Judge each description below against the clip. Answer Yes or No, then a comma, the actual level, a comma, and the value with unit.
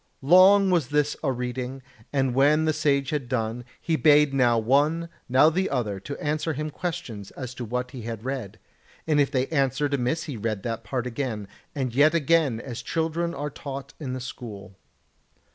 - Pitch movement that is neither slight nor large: Yes, average, 3.8 semitones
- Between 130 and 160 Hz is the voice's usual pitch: Yes, low, 135 Hz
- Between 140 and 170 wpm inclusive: No, average, 180 wpm